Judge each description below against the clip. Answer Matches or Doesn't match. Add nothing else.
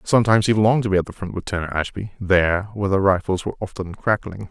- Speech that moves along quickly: Matches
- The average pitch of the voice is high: Doesn't match